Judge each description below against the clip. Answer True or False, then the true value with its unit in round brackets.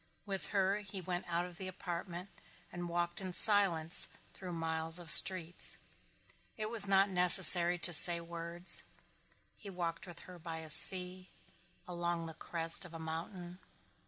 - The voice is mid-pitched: True (175 Hz)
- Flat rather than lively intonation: True (1.8 semitones)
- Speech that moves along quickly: False (155 wpm)